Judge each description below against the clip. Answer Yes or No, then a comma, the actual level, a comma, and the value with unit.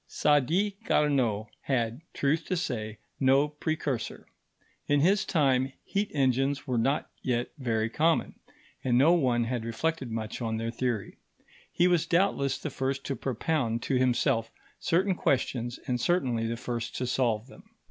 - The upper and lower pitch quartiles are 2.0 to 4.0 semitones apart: No, average, 4.5 semitones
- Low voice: Yes, low, 130 Hz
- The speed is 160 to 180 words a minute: No, average, 150 wpm